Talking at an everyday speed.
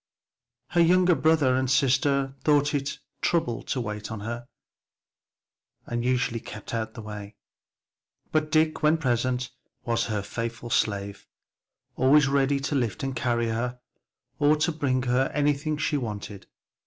Yes: average, 150 wpm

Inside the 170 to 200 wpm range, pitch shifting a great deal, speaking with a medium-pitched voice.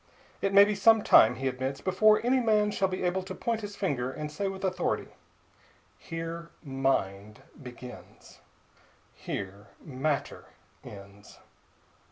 No: slow, 135 wpm; wide, 7.7 semitones; medium, 165 Hz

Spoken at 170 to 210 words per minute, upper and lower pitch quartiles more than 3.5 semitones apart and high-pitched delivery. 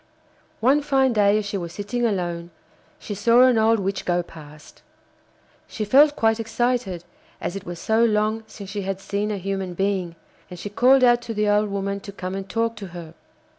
No: average, 200 wpm; average, 3.2 semitones; high, 205 Hz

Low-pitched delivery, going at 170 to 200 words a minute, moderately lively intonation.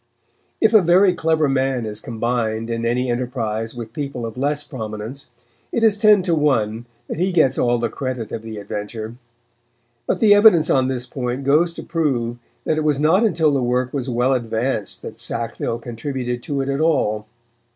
Yes: low, 130 Hz; average, 185 wpm; average, 4.6 semitones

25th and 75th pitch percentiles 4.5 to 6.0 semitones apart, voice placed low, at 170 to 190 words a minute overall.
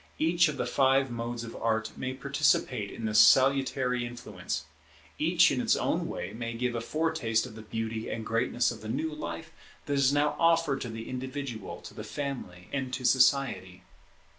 No: average, 3.4 semitones; low, 125 Hz; average, 185 wpm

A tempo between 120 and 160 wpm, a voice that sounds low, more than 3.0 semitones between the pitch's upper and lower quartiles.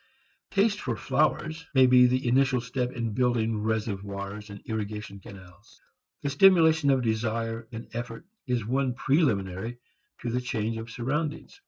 Yes: average, 145 wpm; low, 120 Hz; average, 3.4 semitones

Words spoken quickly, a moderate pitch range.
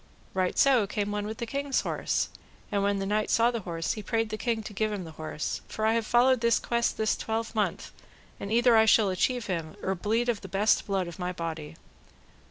Yes: fast, 225 wpm; average, 3.2 semitones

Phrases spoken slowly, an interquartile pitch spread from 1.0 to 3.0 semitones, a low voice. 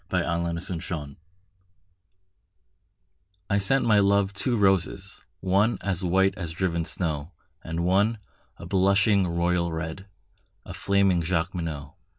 Yes: slow, 120 wpm; average, 2.7 semitones; very low, 95 Hz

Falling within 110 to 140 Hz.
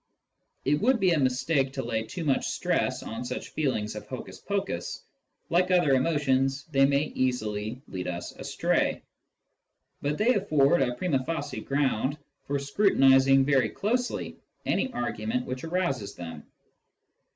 Yes: low, 135 Hz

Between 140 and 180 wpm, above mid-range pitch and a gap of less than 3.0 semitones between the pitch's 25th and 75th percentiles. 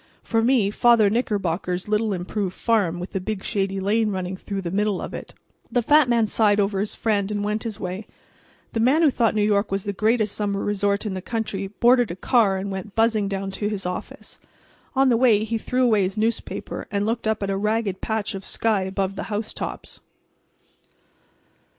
No: average, 200 wpm; high, 210 Hz; narrow, 2.4 semitones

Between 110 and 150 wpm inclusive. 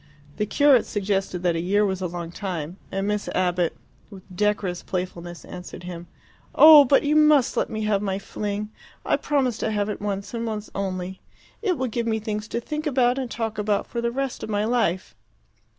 No: average, 200 wpm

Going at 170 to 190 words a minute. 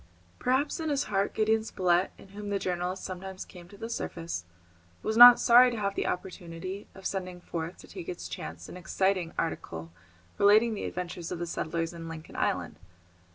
Yes: average, 185 wpm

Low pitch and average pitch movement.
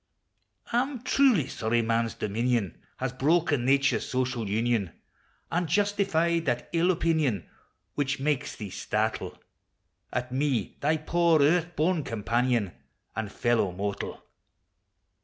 No: low, 130 Hz; wide, 6.3 semitones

